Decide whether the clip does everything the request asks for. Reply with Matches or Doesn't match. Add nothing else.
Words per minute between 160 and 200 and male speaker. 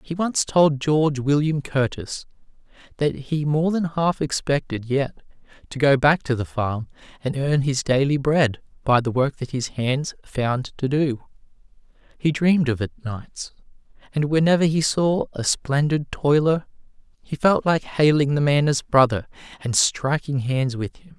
Matches